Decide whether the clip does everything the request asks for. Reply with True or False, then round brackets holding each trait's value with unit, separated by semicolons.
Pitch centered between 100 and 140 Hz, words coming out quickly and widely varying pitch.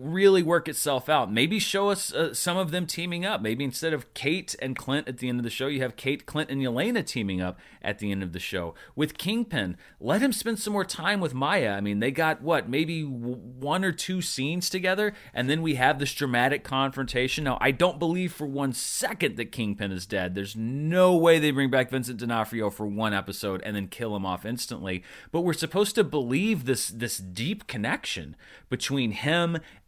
True (135 Hz; 215 wpm; 6.5 semitones)